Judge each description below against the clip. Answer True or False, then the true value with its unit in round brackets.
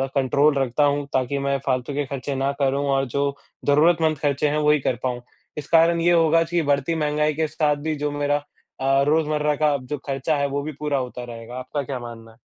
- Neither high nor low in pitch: True (145 Hz)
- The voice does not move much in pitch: True (2.1 semitones)